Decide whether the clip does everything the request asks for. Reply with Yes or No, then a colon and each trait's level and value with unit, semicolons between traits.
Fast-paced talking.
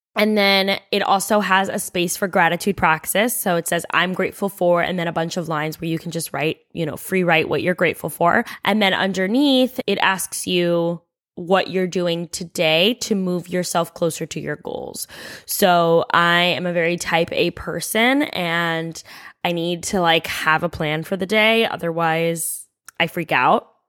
No: average, 190 wpm